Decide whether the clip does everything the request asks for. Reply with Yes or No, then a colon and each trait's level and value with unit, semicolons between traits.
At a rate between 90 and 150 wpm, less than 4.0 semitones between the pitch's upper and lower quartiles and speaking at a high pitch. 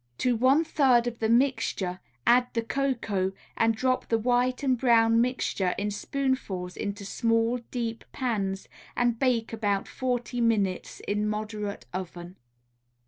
Yes: average, 140 wpm; average, 3.4 semitones; high, 230 Hz